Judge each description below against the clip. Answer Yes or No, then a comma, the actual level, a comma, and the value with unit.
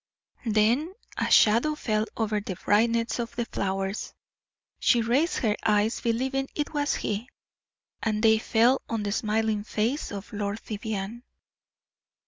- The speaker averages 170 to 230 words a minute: No, slow, 135 wpm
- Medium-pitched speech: No, high, 220 Hz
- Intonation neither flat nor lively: No, narrow, 2.2 semitones